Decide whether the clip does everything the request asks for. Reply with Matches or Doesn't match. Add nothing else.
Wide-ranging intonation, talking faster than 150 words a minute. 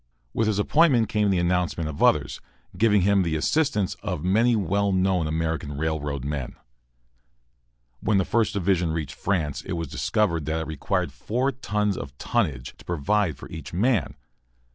Doesn't match